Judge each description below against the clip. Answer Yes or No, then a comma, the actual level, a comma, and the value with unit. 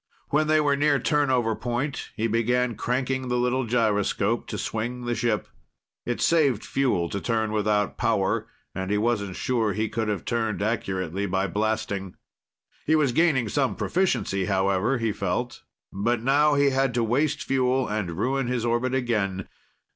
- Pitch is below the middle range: Yes, low, 120 Hz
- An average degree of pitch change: Yes, average, 4.0 semitones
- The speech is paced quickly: No, average, 160 wpm